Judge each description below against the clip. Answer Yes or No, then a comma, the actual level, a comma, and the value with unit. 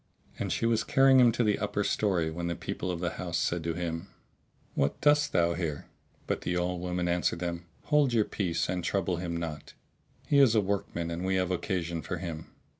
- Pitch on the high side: No, very low, 90 Hz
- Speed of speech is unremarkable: No, fast, 210 wpm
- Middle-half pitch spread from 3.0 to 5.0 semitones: Yes, average, 3.4 semitones